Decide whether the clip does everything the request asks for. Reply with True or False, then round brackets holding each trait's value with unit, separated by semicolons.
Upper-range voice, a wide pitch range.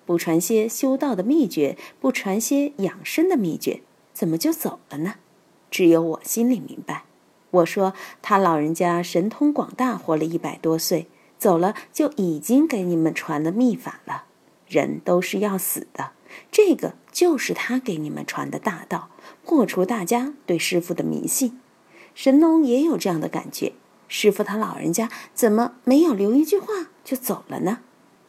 True (215 Hz; 7.9 semitones)